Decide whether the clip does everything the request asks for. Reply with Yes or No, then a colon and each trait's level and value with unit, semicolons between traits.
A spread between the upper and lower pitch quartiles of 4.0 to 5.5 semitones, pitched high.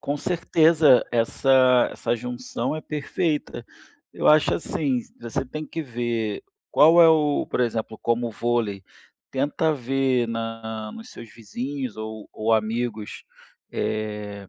No: average, 4.4 semitones; low, 120 Hz